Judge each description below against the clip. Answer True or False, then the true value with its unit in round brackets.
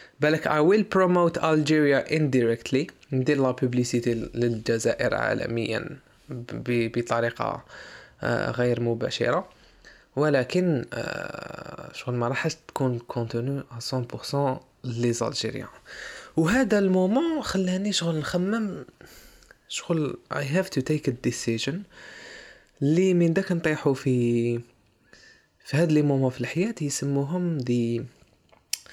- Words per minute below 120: True (105 wpm)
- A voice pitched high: False (140 Hz)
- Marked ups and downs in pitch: True (6.0 semitones)